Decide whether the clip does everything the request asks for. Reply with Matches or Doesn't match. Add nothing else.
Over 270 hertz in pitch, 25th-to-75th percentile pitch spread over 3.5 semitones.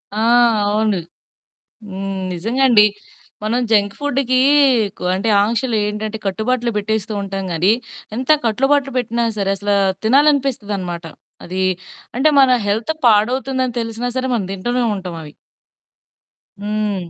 Doesn't match